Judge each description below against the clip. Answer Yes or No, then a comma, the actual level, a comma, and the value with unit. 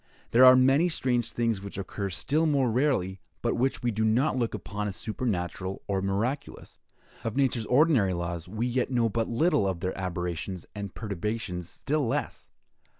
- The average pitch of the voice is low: Yes, low, 115 Hz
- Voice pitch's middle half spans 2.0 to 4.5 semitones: No, average, 4.9 semitones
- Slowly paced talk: No, average, 170 wpm